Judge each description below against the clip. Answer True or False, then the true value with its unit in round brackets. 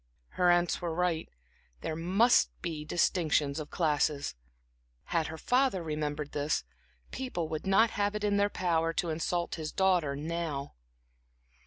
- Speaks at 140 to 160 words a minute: True (145 wpm)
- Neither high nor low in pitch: True (165 Hz)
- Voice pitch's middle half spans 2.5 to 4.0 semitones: True (3.2 semitones)